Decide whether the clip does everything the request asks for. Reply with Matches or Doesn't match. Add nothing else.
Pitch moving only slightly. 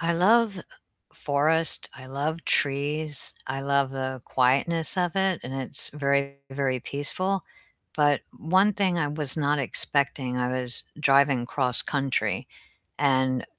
Doesn't match